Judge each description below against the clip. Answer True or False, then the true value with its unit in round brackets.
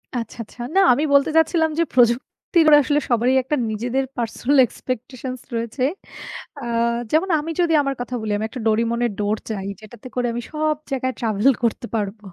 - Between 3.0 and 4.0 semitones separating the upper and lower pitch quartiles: True (3.7 semitones)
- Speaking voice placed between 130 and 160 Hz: False (245 Hz)